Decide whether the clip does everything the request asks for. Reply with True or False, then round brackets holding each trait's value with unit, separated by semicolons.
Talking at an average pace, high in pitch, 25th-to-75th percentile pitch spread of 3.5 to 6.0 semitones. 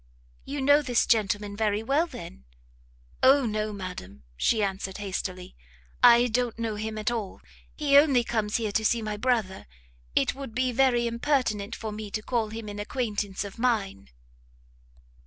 False (160 wpm; 220 Hz; 3.1 semitones)